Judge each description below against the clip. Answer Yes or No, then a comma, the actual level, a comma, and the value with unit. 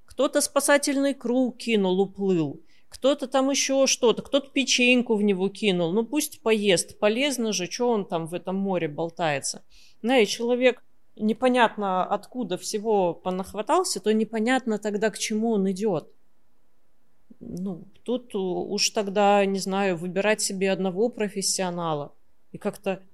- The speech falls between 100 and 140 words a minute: Yes, average, 130 wpm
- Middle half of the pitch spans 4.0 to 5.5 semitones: Yes, average, 4.3 semitones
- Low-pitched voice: No, high, 210 Hz